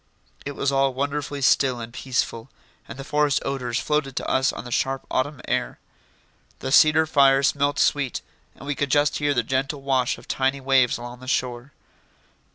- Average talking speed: Yes, average, 180 wpm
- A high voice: No, low, 135 Hz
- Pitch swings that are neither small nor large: No, narrow, 1.8 semitones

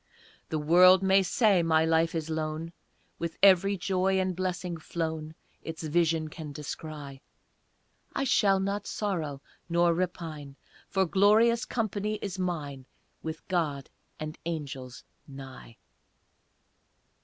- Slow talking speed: Yes, slow, 120 wpm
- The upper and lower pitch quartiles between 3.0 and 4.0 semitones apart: Yes, average, 3.5 semitones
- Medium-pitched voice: Yes, medium, 165 Hz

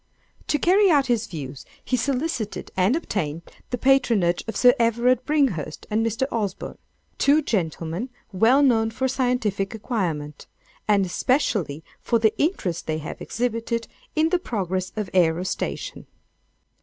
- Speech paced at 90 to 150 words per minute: Yes, slow, 135 wpm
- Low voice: No, high, 225 Hz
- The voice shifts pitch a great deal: Yes, wide, 5.9 semitones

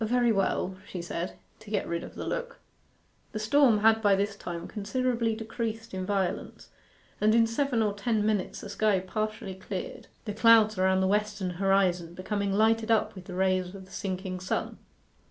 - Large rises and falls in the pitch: No, average, 2.9 semitones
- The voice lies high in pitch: Yes, high, 205 Hz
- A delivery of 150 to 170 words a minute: No, average, 180 wpm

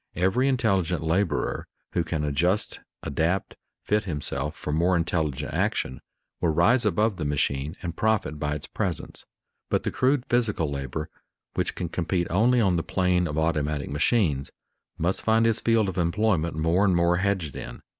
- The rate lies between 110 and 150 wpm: No, average, 165 wpm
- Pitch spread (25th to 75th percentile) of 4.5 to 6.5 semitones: Yes, average, 4.9 semitones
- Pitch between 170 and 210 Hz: No, very low, 85 Hz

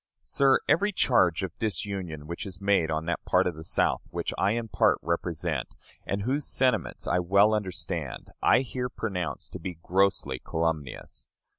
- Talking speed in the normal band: Yes, average, 165 wpm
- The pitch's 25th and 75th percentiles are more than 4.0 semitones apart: Yes, average, 4.6 semitones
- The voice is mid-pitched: No, very low, 90 Hz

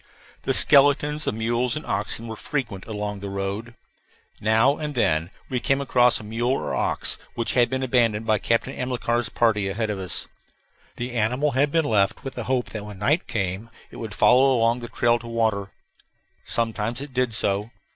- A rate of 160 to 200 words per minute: Yes, average, 185 wpm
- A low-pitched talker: Yes, low, 115 Hz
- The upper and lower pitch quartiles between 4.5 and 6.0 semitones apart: No, average, 3.3 semitones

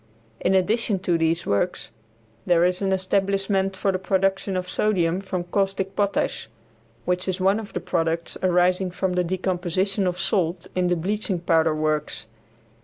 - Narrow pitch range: Yes, narrow, 1.8 semitones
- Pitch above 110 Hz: Yes, medium, 185 Hz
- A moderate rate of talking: Yes, average, 160 wpm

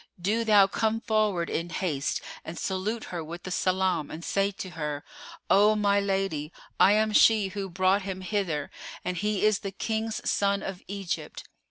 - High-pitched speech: Yes, high, 195 Hz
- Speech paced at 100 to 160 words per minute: No, average, 170 wpm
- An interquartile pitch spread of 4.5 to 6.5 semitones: No, average, 3.0 semitones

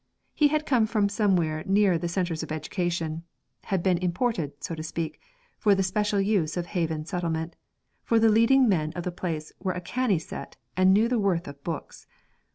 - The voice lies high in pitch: No, medium, 180 Hz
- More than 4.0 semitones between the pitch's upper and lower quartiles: Yes, average, 4.4 semitones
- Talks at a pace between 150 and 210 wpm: Yes, average, 190 wpm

